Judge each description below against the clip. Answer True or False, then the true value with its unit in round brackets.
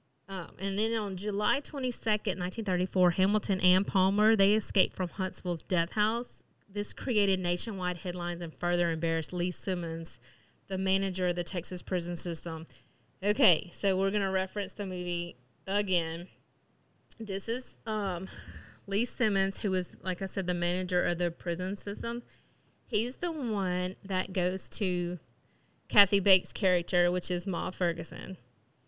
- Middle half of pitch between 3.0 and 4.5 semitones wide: False (2.4 semitones)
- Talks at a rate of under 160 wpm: True (145 wpm)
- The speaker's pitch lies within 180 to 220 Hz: True (185 Hz)